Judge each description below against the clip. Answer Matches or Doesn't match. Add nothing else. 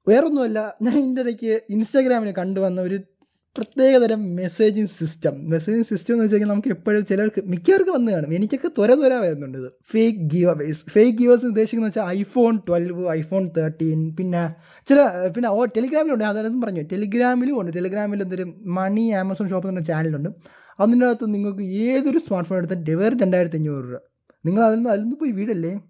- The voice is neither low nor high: Doesn't match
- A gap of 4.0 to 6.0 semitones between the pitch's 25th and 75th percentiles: Matches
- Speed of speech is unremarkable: Doesn't match